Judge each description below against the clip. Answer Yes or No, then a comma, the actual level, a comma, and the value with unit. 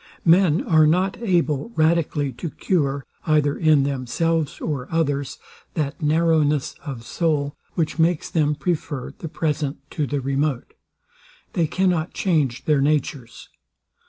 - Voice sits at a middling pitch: Yes, medium, 150 Hz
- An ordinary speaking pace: No, slow, 130 wpm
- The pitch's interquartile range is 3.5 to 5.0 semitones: No, narrow, 2.6 semitones